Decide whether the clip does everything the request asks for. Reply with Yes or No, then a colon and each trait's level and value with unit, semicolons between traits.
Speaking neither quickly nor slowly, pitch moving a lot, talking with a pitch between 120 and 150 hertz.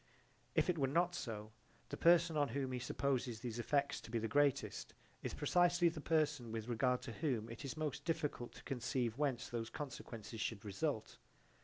No: average, 185 wpm; average, 4.5 semitones; low, 135 Hz